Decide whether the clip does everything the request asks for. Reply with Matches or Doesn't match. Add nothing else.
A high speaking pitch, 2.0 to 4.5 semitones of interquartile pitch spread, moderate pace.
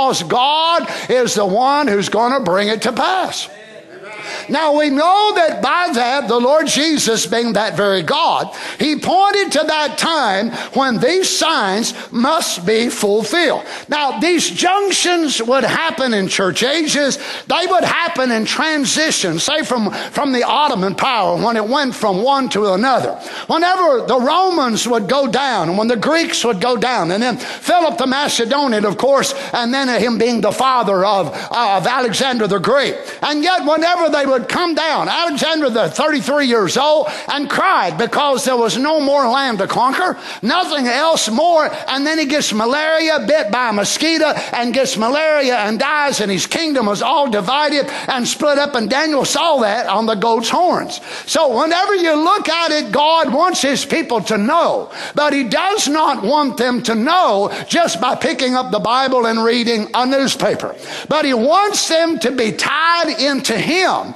Doesn't match